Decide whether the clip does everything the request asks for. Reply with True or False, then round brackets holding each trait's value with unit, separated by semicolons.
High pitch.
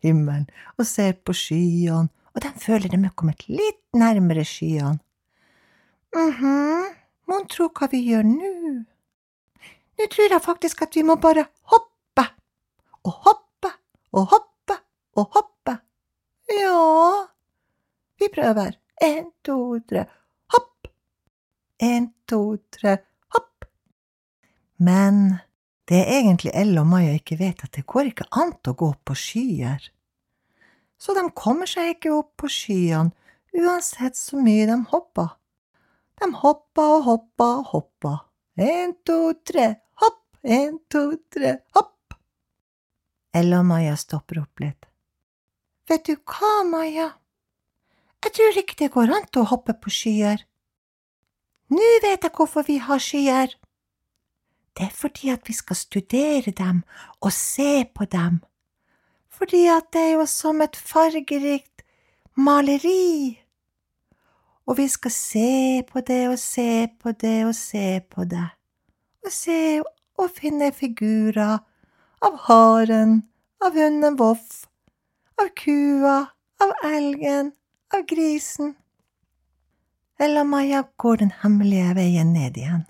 True (260 Hz)